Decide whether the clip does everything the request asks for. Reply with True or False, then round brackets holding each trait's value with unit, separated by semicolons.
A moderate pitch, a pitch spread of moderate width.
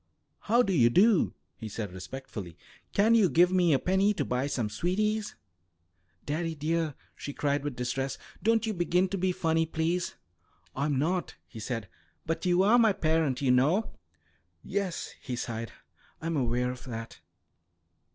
False (160 Hz; 6.7 semitones)